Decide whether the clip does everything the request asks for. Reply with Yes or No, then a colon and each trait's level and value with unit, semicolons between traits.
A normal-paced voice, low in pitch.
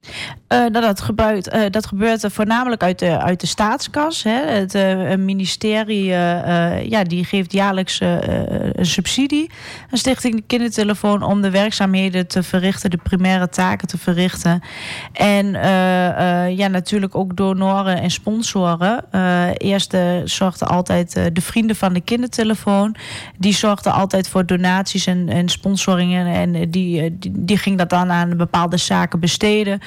No: average, 160 wpm; high, 190 Hz